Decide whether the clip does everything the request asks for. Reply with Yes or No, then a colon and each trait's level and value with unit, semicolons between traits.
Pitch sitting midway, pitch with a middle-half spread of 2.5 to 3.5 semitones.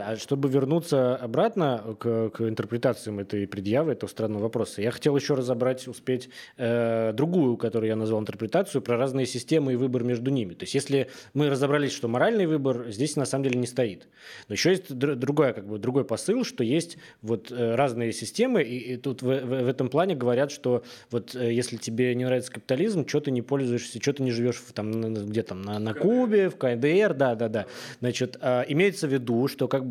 No: low, 125 Hz; average, 3.1 semitones